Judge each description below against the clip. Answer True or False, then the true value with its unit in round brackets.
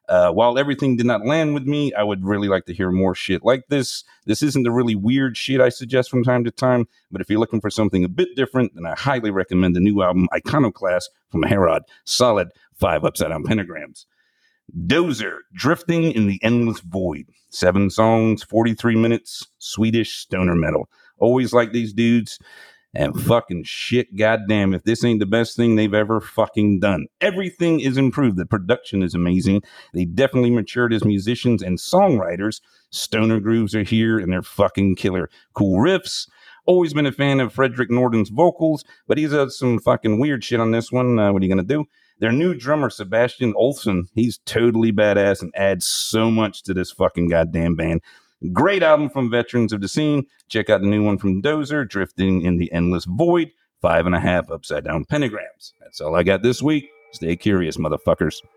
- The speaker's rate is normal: True (190 wpm)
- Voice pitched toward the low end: True (115 Hz)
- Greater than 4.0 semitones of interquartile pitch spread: True (4.6 semitones)